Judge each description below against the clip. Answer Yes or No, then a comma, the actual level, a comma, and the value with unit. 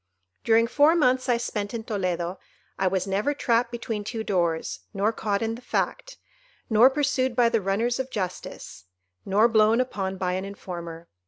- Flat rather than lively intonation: No, average, 4.1 semitones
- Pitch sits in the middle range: No, high, 220 Hz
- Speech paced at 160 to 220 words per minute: Yes, average, 170 wpm